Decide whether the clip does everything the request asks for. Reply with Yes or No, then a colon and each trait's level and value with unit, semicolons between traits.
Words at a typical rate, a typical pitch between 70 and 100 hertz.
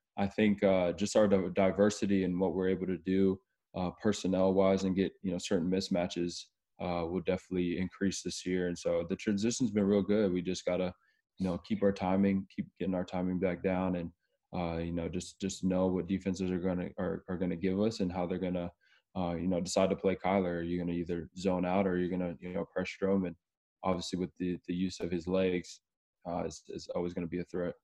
No: fast, 225 wpm; very low, 90 Hz